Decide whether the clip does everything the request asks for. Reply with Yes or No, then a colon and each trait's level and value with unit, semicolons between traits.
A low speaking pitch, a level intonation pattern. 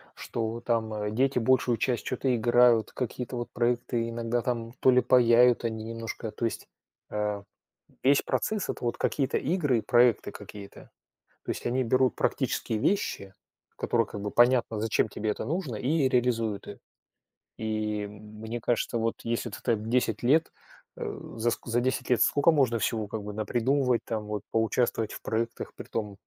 Yes: low, 115 Hz; narrow, 2.2 semitones